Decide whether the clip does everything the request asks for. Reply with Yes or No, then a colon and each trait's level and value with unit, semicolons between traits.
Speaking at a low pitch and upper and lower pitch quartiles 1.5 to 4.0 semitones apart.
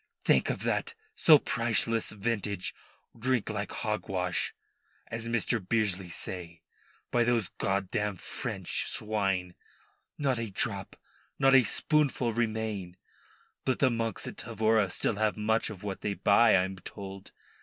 Yes: low, 110 Hz; average, 3.2 semitones